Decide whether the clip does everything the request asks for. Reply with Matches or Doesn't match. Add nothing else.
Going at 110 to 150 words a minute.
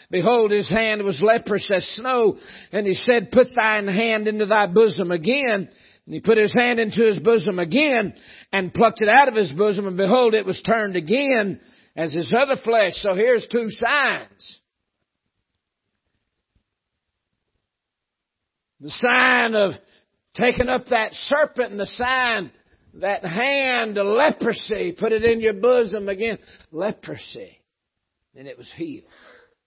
Matches